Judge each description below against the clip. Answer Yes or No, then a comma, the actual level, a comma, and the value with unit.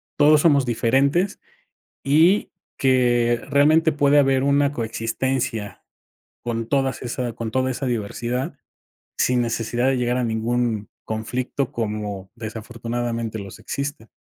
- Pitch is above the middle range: No, low, 120 Hz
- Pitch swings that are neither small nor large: Yes, average, 3.3 semitones